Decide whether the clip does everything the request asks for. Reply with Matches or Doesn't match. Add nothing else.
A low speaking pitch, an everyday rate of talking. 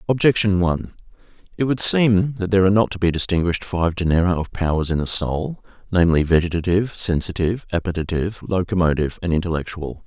Matches